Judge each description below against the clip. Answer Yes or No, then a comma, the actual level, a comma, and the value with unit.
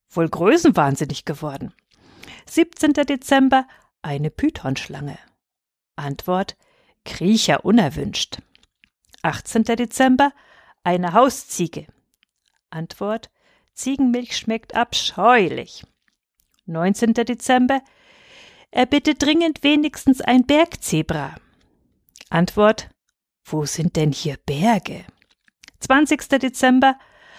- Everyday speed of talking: No, slow, 75 wpm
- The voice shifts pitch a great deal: Yes, wide, 8.5 semitones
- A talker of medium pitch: No, high, 235 Hz